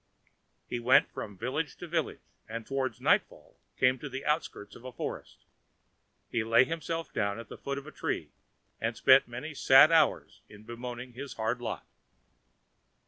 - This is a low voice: Yes, low, 125 Hz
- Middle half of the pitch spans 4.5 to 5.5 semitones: No, average, 3.3 semitones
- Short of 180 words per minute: Yes, average, 170 wpm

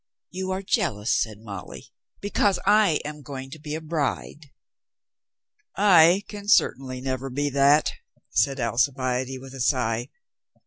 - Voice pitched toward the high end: No, medium, 140 Hz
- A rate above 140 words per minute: No, slow, 135 wpm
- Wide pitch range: No, average, 4.8 semitones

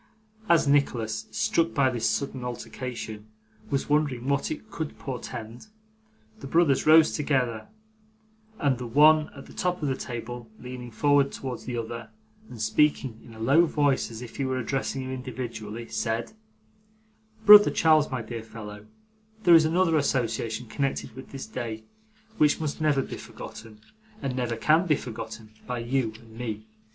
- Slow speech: No, average, 160 wpm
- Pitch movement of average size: Yes, average, 4.3 semitones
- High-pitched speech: No, low, 130 Hz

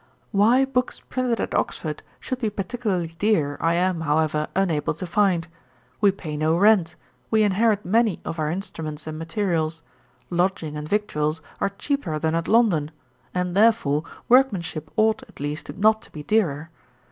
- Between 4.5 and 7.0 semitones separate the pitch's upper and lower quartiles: Yes, average, 5.3 semitones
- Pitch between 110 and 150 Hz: No, medium, 180 Hz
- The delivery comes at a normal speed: Yes, average, 160 wpm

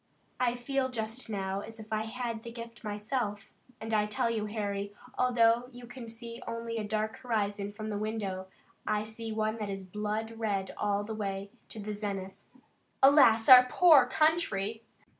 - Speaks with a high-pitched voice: Yes, high, 220 Hz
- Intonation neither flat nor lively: No, narrow, 2.1 semitones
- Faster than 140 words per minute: Yes, average, 175 wpm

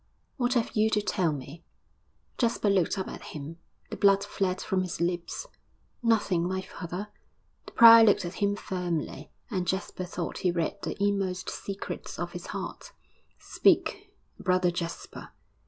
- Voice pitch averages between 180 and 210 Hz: Yes, medium, 185 Hz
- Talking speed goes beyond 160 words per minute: No, average, 155 wpm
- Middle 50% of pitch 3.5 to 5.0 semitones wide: No, average, 2.8 semitones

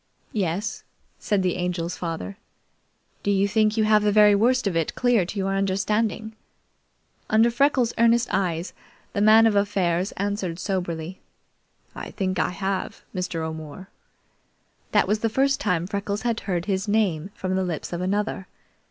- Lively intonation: No, average, 3.1 semitones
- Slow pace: No, average, 155 wpm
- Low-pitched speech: No, high, 195 Hz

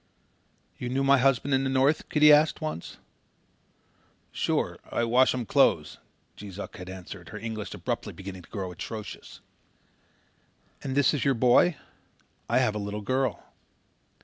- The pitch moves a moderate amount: Yes, average, 5.0 semitones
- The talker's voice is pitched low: Yes, low, 120 Hz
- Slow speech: No, average, 150 wpm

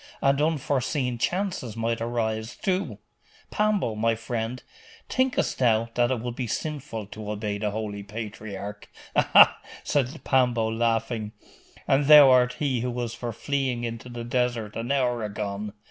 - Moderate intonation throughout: Yes, average, 3.0 semitones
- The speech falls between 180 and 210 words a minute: No, average, 145 wpm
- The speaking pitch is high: No, low, 120 Hz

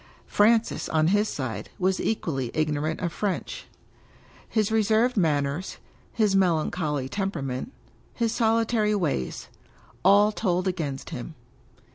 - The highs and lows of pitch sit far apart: Yes, wide, 5.9 semitones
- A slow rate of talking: Yes, slow, 120 wpm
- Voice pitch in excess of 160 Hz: Yes, medium, 185 Hz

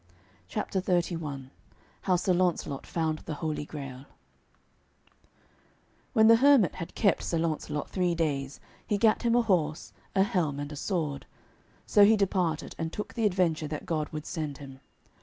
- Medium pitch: Yes, medium, 165 Hz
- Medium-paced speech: Yes, average, 160 wpm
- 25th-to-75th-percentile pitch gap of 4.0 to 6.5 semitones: Yes, average, 4.4 semitones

